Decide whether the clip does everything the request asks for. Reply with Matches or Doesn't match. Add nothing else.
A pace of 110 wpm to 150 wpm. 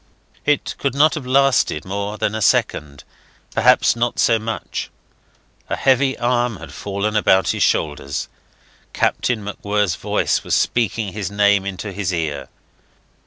Matches